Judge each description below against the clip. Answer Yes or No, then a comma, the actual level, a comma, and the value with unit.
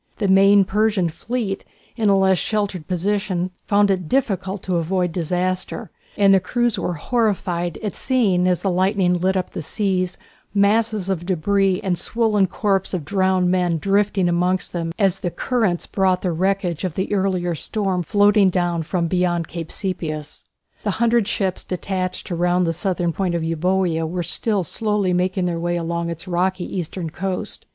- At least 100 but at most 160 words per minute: No, average, 170 wpm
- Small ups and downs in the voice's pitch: Yes, narrow, 2.3 semitones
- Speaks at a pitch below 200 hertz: Yes, medium, 185 Hz